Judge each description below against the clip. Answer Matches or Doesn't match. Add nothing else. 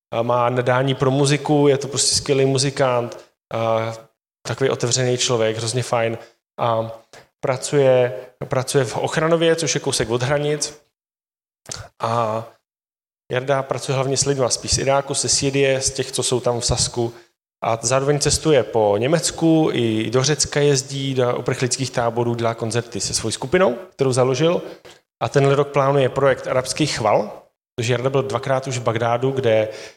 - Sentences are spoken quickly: Doesn't match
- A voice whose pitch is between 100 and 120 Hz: Doesn't match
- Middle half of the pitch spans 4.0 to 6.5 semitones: Doesn't match